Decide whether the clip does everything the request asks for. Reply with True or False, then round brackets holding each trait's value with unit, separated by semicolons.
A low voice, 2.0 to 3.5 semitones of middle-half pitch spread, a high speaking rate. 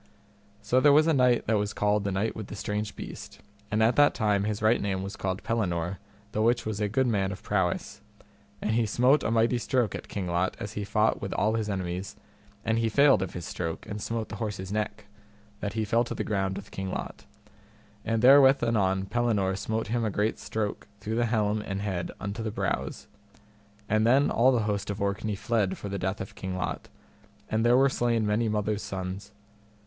True (105 Hz; 2.6 semitones; 215 wpm)